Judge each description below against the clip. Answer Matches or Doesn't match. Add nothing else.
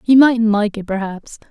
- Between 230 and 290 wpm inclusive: Doesn't match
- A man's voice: Doesn't match